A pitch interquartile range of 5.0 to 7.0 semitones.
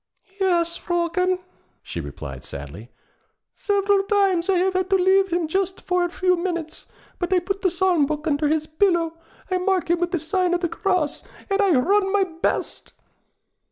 No: average, 2.7 semitones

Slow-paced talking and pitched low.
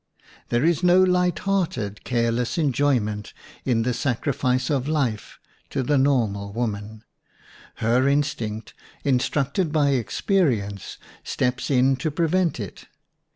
Yes: slow, 115 wpm; low, 130 Hz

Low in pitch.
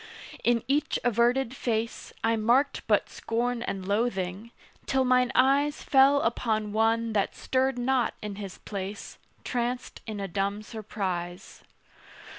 No: high, 230 Hz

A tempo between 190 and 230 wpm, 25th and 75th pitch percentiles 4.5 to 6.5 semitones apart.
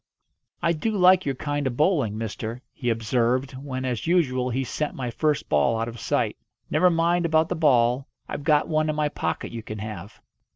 Yes: average, 200 wpm; average, 4.8 semitones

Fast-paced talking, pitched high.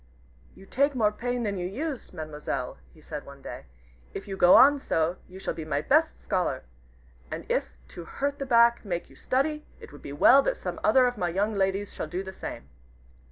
Yes: fast, 210 wpm; high, 195 Hz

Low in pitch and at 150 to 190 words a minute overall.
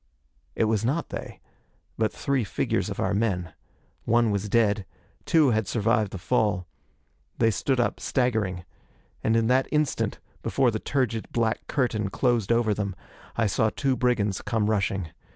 Yes: low, 110 Hz; average, 155 wpm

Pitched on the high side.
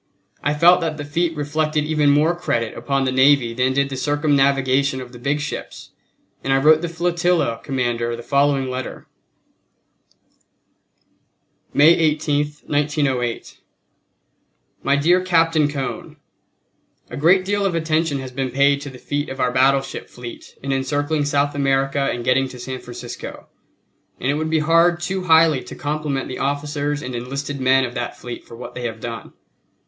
No: medium, 140 Hz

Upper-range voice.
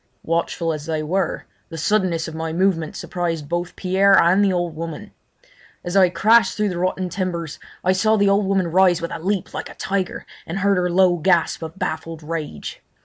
No: medium, 175 Hz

